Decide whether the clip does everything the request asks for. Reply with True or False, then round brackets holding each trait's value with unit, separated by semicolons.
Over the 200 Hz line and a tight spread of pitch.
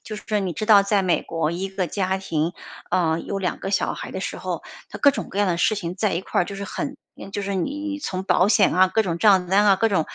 False (195 Hz; 2.3 semitones)